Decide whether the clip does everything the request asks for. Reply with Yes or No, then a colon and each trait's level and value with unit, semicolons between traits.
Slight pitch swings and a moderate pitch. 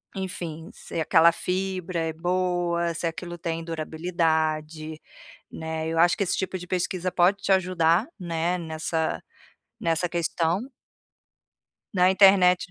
Yes: narrow, 2.0 semitones; medium, 170 Hz